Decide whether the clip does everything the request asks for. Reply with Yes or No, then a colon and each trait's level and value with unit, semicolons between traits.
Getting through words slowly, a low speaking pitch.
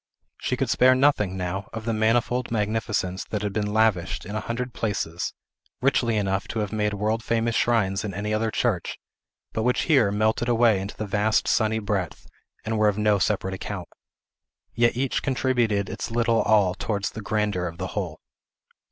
No: average, 180 wpm; low, 110 Hz